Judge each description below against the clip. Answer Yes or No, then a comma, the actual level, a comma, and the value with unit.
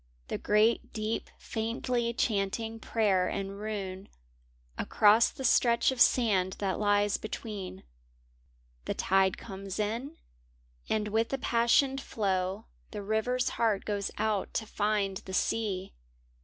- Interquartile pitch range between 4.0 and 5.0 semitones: No, average, 2.7 semitones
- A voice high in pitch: Yes, high, 215 Hz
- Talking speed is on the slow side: Yes, slow, 125 wpm